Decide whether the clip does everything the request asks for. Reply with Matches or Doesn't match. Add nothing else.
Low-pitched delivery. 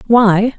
Doesn't match